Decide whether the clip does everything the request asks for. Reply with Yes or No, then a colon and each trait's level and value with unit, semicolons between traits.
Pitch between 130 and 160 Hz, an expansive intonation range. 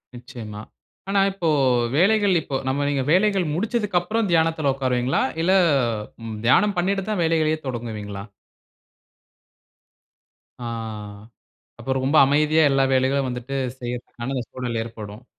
Yes: medium, 140 Hz; wide, 6.2 semitones